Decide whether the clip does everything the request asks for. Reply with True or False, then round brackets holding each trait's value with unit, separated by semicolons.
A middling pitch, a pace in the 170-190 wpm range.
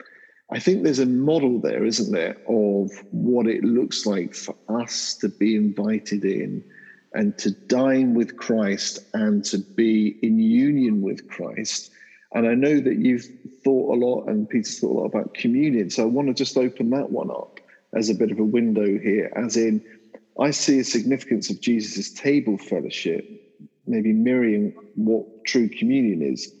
False (125 Hz; 175 wpm)